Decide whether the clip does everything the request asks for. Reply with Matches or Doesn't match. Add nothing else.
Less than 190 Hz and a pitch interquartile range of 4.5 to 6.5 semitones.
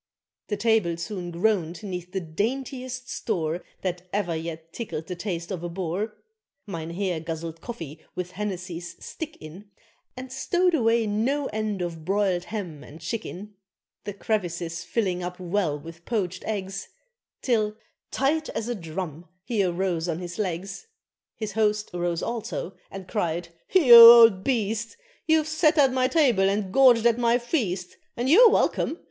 Doesn't match